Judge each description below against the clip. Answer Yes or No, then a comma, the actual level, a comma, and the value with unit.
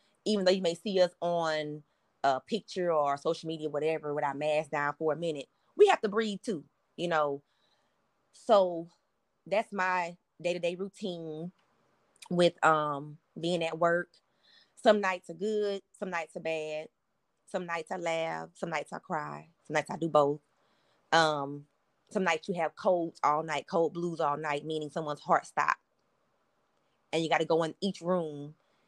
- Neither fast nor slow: Yes, average, 170 wpm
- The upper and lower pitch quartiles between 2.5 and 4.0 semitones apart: Yes, average, 3.1 semitones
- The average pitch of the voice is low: No, medium, 165 Hz